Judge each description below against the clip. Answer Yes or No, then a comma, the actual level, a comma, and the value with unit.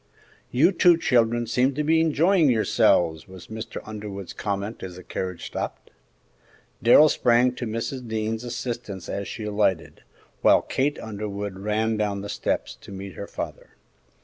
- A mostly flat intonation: No, average, 3.8 semitones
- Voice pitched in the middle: No, low, 110 Hz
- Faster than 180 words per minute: No, average, 150 wpm